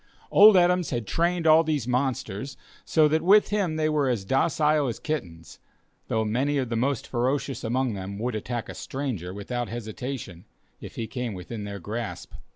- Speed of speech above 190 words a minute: No, average, 175 wpm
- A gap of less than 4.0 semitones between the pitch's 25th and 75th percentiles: No, wide, 5.6 semitones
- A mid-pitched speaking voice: No, low, 125 Hz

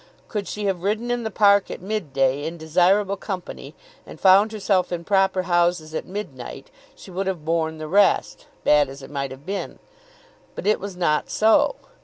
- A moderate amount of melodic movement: Yes, average, 4.2 semitones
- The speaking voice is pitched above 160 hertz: Yes, medium, 185 Hz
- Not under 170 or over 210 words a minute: Yes, average, 190 wpm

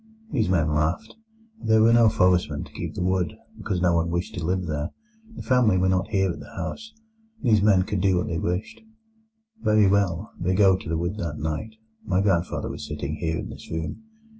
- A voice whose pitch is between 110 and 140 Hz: No, very low, 90 Hz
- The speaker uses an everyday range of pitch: Yes, average, 3.7 semitones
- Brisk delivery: Yes, fast, 210 wpm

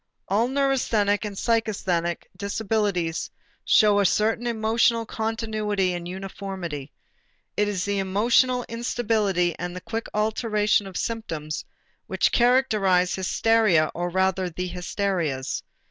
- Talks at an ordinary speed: No, slow, 115 wpm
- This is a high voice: Yes, high, 205 Hz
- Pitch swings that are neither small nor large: Yes, average, 3.7 semitones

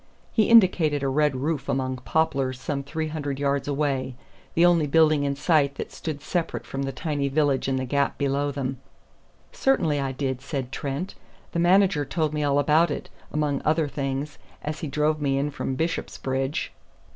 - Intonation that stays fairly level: Yes, narrow, 2.3 semitones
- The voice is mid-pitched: Yes, medium, 145 Hz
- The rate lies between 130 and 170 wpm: No, average, 180 wpm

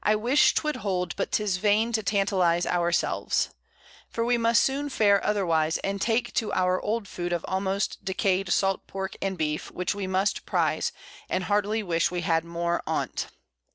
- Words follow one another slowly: No, average, 185 wpm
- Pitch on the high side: Yes, high, 195 Hz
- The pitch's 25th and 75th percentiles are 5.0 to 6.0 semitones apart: No, average, 3.2 semitones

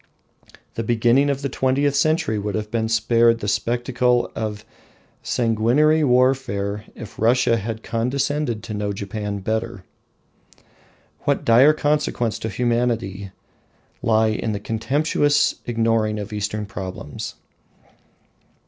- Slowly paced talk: Yes, slow, 115 wpm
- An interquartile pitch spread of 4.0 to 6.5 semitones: No, average, 3.2 semitones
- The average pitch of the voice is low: Yes, low, 115 Hz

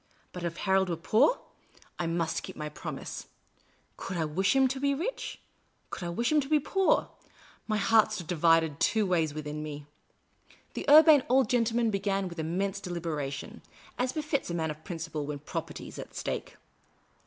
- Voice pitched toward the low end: No, medium, 185 Hz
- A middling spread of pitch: No, wide, 6.8 semitones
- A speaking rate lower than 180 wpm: No, average, 185 wpm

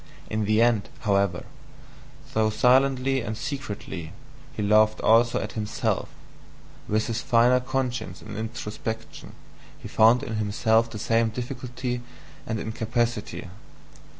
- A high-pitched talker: No, low, 115 Hz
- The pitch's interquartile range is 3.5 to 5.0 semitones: No, narrow, 2.4 semitones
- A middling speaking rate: No, slow, 120 wpm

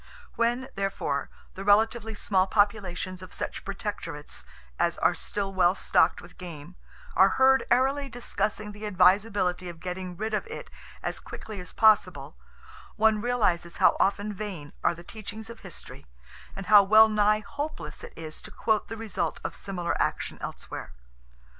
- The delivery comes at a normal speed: Yes, average, 155 wpm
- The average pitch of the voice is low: No, high, 200 Hz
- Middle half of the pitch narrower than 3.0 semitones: No, average, 3.3 semitones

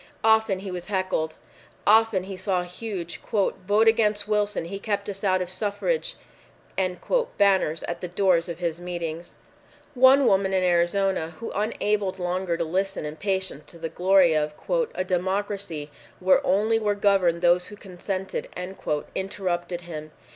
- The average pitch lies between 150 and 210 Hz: Yes, high, 190 Hz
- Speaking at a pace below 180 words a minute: Yes, average, 145 wpm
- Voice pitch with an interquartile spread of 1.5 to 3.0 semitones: Yes, average, 2.7 semitones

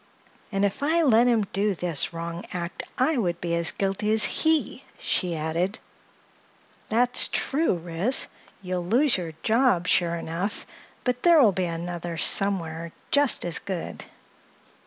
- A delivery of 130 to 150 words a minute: Yes, average, 145 wpm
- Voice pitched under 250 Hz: Yes, high, 190 Hz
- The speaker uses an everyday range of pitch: No, wide, 5.8 semitones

